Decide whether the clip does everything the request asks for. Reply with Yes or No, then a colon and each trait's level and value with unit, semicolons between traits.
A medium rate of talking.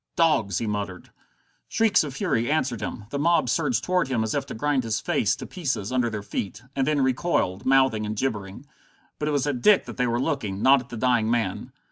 No: fast, 220 wpm